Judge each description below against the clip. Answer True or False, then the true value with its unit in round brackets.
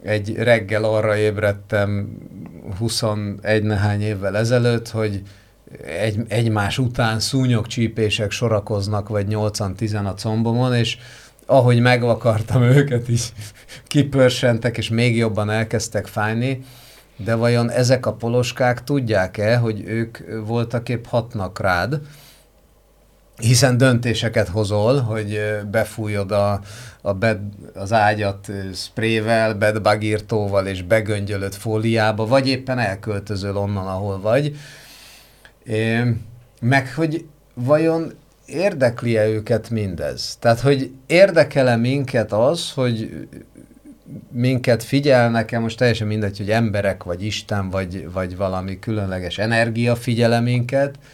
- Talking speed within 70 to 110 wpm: True (105 wpm)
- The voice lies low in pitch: True (110 Hz)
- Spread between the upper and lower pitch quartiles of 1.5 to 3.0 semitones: True (2.6 semitones)